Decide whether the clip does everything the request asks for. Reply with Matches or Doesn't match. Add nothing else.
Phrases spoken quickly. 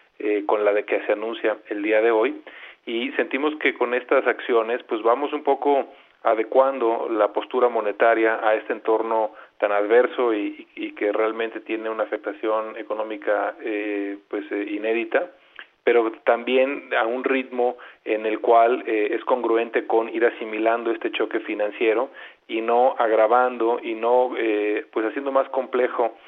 Doesn't match